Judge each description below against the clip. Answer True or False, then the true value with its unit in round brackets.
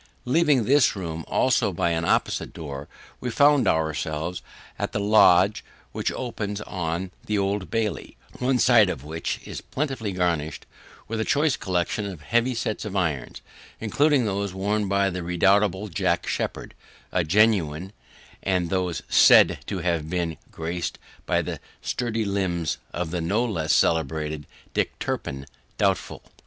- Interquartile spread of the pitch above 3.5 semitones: True (4.7 semitones)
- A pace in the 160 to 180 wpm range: False (145 wpm)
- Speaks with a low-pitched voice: True (95 Hz)